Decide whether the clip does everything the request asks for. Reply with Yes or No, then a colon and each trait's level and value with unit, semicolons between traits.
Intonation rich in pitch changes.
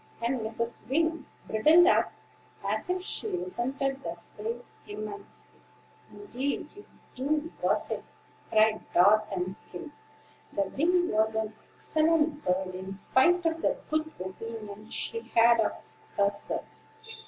Yes: wide, 6.8 semitones